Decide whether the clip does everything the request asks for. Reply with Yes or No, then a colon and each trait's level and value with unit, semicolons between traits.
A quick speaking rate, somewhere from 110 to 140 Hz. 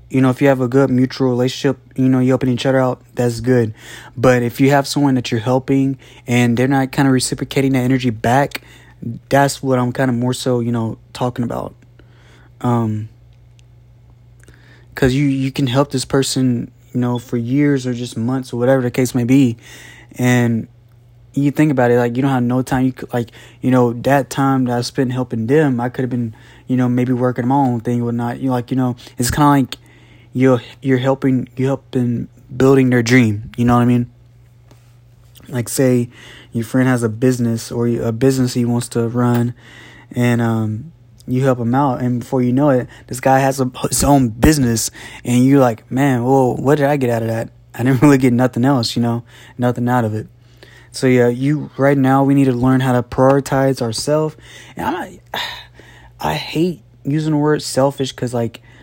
Yes: fast, 210 wpm; low, 125 Hz